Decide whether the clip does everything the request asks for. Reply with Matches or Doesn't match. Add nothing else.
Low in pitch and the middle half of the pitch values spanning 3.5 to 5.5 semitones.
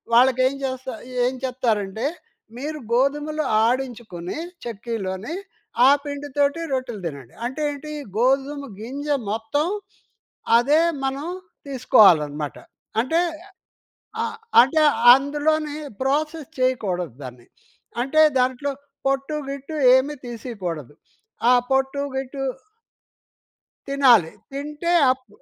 Doesn't match